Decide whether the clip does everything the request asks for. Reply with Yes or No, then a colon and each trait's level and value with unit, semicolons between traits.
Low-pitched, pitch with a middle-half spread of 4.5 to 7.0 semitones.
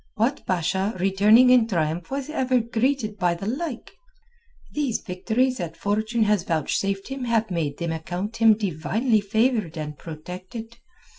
No: high, 210 Hz; average, 4.9 semitones